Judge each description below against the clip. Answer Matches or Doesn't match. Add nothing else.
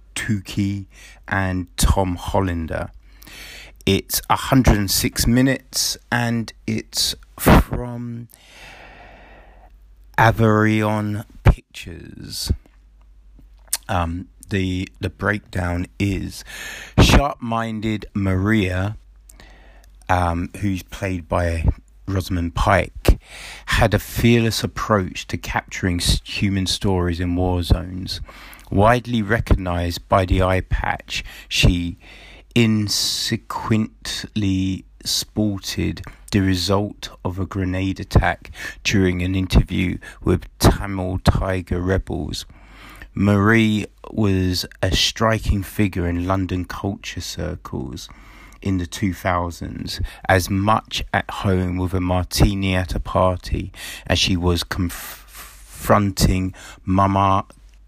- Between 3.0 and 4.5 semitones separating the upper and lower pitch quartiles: Doesn't match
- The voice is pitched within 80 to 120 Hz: Matches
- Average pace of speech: Doesn't match